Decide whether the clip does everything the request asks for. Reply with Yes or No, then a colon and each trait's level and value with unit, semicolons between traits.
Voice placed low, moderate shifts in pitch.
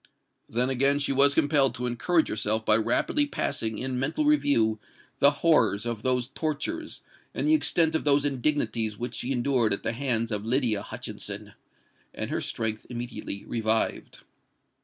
Yes: low, 125 Hz; average, 4.2 semitones